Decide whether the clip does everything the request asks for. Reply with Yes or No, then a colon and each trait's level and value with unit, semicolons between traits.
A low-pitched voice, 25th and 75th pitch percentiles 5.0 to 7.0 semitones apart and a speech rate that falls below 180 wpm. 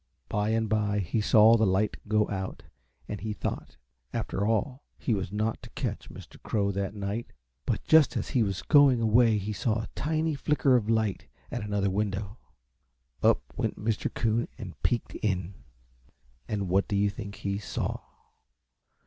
No: low, 105 Hz; narrow, 2.4 semitones; average, 170 wpm